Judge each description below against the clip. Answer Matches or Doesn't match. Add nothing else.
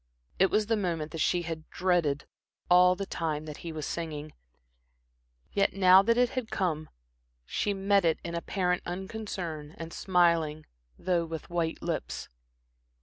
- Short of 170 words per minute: Matches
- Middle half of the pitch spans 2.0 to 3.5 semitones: Matches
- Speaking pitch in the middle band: Matches